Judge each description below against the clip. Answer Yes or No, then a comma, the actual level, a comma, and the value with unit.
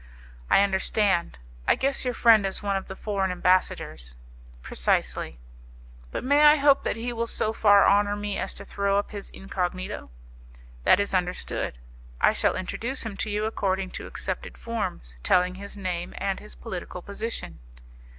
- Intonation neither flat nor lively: Yes, average, 3.0 semitones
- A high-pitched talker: Yes, high, 200 Hz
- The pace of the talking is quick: No, average, 165 wpm